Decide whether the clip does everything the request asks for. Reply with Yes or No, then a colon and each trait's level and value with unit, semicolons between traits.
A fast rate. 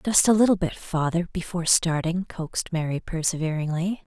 No: average, 145 wpm